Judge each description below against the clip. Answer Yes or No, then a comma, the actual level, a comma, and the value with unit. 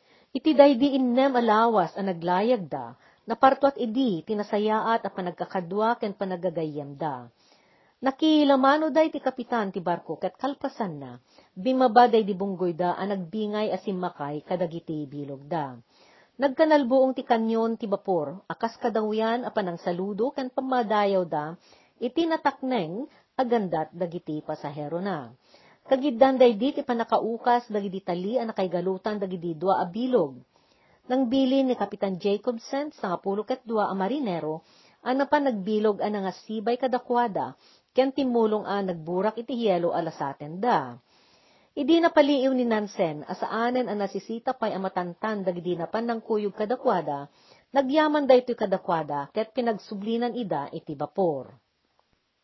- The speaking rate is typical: Yes, average, 135 wpm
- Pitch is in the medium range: No, high, 215 Hz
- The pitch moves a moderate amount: No, wide, 5.7 semitones